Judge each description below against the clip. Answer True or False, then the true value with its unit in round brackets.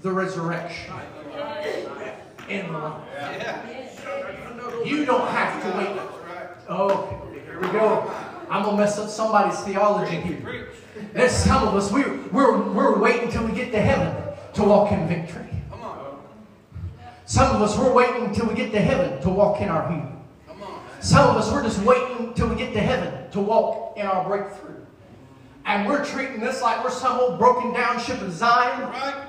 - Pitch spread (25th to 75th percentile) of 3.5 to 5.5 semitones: True (4.1 semitones)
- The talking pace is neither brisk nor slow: True (170 wpm)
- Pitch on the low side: False (215 Hz)